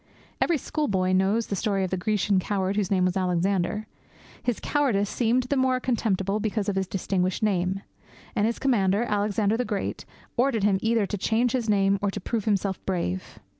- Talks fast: No, average, 185 wpm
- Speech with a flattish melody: No, average, 3.0 semitones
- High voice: Yes, high, 205 Hz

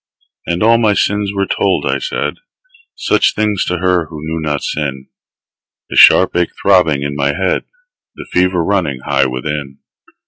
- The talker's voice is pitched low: Yes, very low, 85 Hz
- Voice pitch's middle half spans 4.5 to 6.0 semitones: Yes, average, 5.1 semitones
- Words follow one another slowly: No, average, 165 wpm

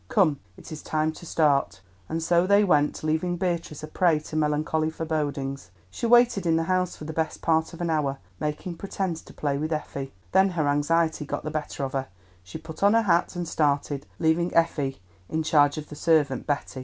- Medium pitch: Yes, medium, 160 Hz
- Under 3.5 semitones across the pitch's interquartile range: Yes, narrow, 2.6 semitones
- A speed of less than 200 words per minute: No, fast, 205 wpm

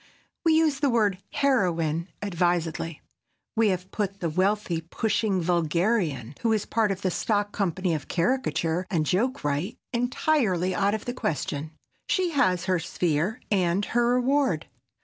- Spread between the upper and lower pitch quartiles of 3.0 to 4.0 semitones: No, average, 5.3 semitones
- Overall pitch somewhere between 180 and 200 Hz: Yes, high, 190 Hz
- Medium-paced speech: Yes, average, 150 wpm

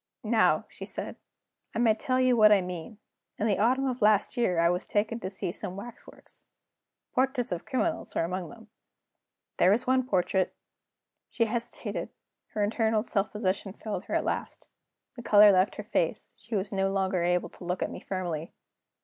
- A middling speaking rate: Yes, average, 185 wpm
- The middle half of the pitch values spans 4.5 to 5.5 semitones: No, average, 4.0 semitones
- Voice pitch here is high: Yes, high, 210 Hz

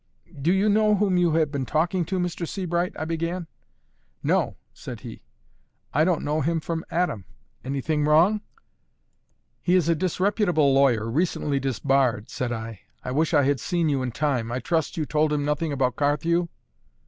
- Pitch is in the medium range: Yes, medium, 155 Hz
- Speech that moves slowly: No, average, 170 wpm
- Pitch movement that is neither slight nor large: Yes, average, 4.0 semitones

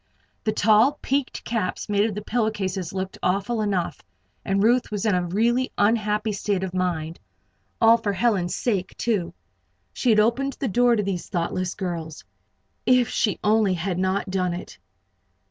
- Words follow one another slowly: No, average, 165 wpm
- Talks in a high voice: Yes, high, 205 Hz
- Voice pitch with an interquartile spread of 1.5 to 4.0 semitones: Yes, average, 3.5 semitones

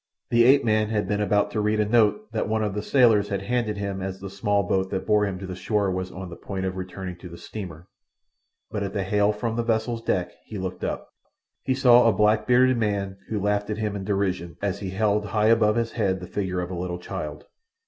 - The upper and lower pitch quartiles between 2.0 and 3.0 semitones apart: Yes, narrow, 2.4 semitones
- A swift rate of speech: Yes, fast, 245 wpm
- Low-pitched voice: Yes, low, 105 Hz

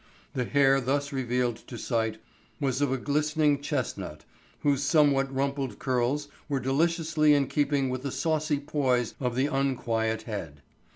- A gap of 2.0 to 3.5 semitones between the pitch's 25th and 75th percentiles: Yes, average, 2.7 semitones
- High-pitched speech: No, low, 135 Hz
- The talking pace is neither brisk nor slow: Yes, average, 150 wpm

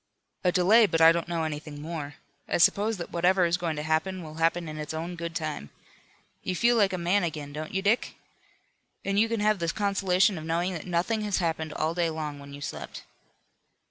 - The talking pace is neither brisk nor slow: No, fast, 215 wpm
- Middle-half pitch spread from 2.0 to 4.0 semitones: Yes, average, 3.3 semitones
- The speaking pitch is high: No, medium, 170 Hz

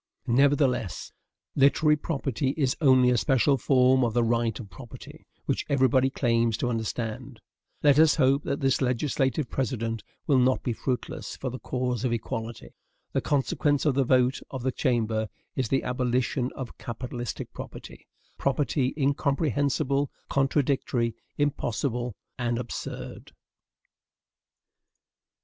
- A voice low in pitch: Yes, low, 130 Hz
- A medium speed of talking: No, slow, 125 wpm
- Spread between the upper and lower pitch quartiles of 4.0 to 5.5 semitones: No, narrow, 2.5 semitones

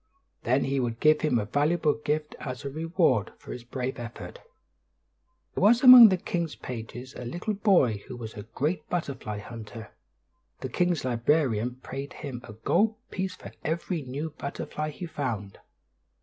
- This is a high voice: No, medium, 140 Hz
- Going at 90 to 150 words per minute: No, average, 165 wpm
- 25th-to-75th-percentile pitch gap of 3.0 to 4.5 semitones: No, wide, 5.5 semitones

